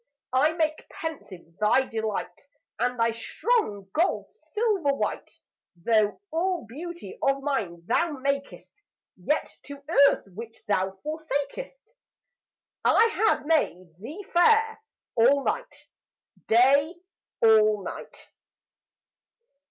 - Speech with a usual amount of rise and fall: No, wide, 7.6 semitones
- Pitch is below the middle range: No, very high, 280 Hz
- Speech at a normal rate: No, slow, 105 wpm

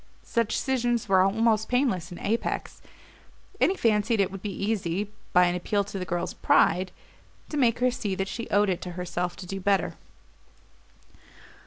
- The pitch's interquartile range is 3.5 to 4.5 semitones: Yes, average, 3.9 semitones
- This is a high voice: Yes, high, 200 Hz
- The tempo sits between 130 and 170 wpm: No, average, 180 wpm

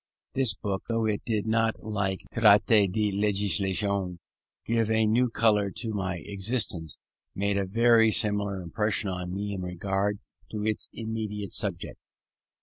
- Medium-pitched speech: No, low, 105 Hz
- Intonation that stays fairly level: Yes, narrow, 2.3 semitones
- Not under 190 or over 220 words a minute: No, average, 145 wpm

